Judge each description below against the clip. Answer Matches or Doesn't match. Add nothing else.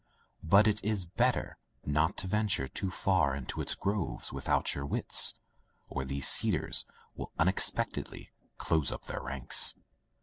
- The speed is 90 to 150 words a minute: Matches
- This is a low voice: Matches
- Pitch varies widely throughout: Matches